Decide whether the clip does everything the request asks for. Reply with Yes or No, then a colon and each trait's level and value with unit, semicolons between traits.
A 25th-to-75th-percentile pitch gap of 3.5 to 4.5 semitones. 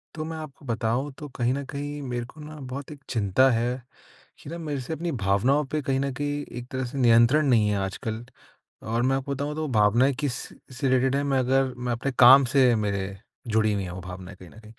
Yes: average, 3.8 semitones